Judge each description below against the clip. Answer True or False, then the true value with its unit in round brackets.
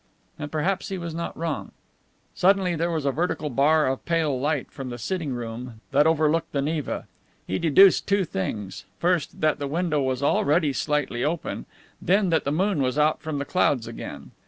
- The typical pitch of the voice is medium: True (150 Hz)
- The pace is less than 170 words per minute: False (185 wpm)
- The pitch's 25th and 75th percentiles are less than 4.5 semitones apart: True (3.6 semitones)